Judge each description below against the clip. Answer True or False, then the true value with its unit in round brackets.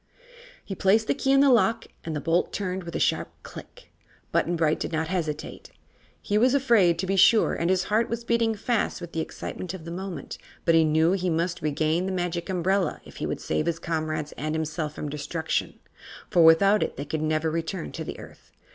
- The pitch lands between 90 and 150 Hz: False (175 Hz)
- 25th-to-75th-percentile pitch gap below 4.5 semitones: True (3.7 semitones)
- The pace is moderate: False (215 wpm)